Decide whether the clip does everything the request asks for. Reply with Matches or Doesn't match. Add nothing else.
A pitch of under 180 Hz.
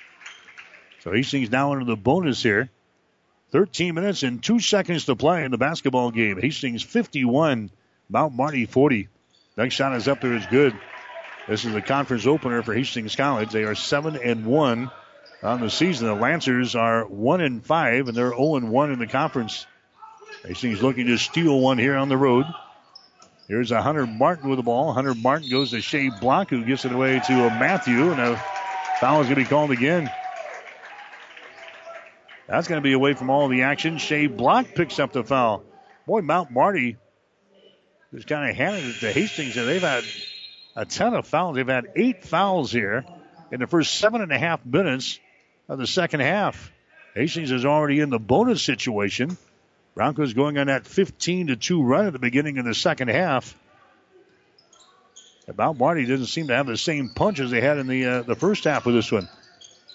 Matches